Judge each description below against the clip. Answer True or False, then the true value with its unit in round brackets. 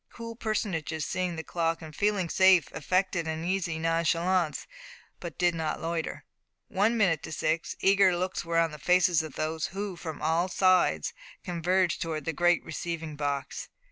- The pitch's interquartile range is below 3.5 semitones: True (2.5 semitones)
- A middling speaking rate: True (165 wpm)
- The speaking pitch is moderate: True (170 Hz)